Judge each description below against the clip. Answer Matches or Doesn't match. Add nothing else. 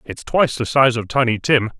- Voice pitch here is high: Doesn't match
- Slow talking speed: Doesn't match